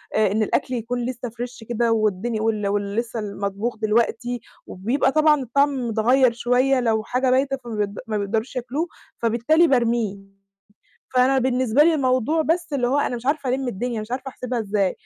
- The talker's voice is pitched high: Yes, high, 240 Hz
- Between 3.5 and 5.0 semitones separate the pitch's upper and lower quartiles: No, average, 3.1 semitones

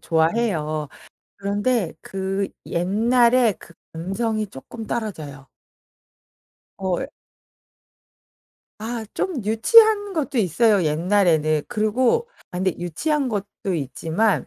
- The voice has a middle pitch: No, high, 205 Hz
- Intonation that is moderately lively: No, wide, 5.7 semitones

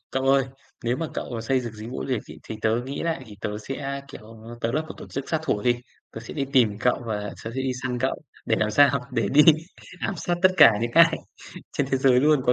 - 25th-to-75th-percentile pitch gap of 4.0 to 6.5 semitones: No, average, 3.5 semitones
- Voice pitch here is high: No, low, 125 Hz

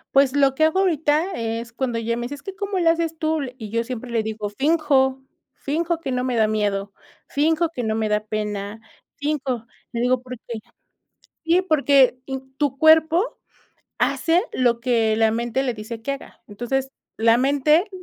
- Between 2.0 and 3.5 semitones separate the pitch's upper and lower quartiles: No, average, 5.3 semitones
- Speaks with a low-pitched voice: No, very high, 260 Hz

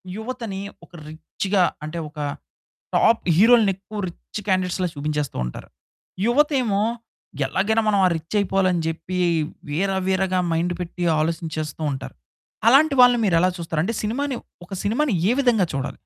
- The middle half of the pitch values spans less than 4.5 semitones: No, average, 5.2 semitones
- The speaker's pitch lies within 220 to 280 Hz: No, high, 190 Hz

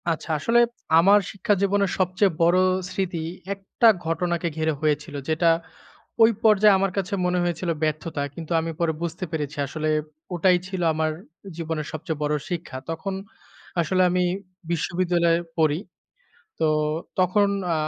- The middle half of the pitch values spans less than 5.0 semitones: Yes, average, 2.8 semitones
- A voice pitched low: No, medium, 170 Hz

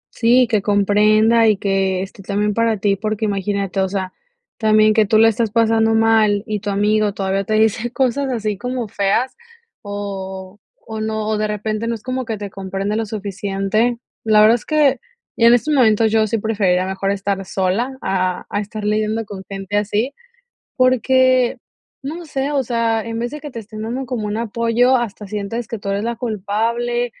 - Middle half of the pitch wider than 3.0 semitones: No, narrow, 2.5 semitones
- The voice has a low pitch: No, high, 215 Hz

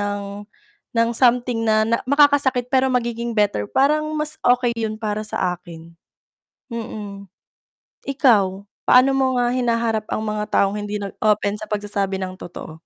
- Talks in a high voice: Yes, high, 225 Hz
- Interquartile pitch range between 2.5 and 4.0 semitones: Yes, average, 3.4 semitones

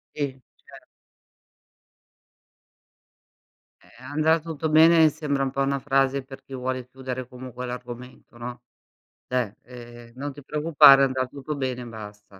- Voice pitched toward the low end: Yes, low, 130 Hz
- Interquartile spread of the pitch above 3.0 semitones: No, narrow, 2.4 semitones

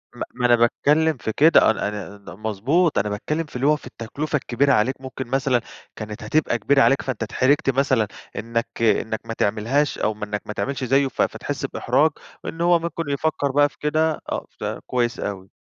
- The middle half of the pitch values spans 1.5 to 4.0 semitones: No, average, 4.8 semitones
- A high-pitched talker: No, low, 130 Hz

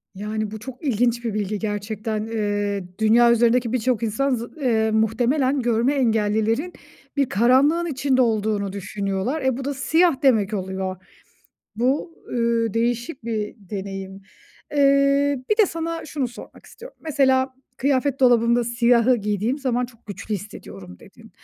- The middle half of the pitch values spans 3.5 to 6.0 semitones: Yes, average, 3.8 semitones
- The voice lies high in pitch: Yes, high, 235 Hz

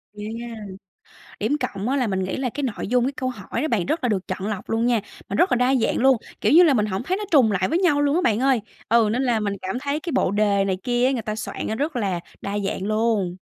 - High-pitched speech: Yes, high, 230 Hz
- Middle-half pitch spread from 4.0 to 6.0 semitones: Yes, average, 4.6 semitones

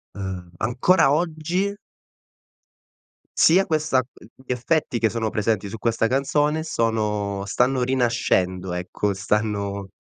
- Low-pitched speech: Yes, low, 115 Hz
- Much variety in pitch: Yes, wide, 5.8 semitones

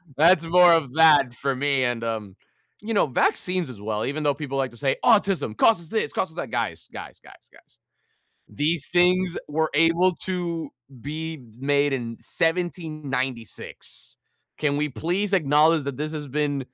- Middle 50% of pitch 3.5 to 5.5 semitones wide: Yes, average, 4.1 semitones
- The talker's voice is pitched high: No, medium, 150 Hz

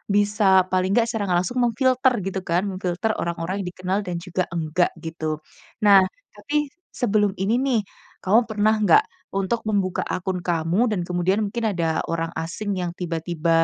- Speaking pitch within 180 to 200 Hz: Yes, medium, 185 Hz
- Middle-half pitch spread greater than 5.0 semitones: No, average, 3.6 semitones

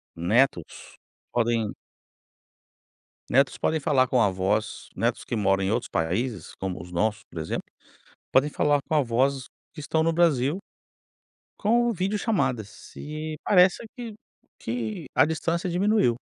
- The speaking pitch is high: No, low, 130 Hz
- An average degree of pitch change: No, wide, 7.4 semitones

